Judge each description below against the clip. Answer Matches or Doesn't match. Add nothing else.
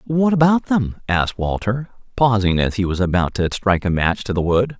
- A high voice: Doesn't match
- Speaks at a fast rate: Matches